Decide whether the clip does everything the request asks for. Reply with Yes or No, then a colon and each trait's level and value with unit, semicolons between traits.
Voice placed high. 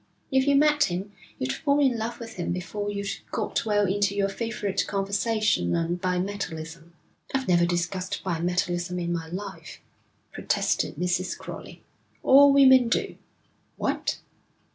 Yes: high, 195 Hz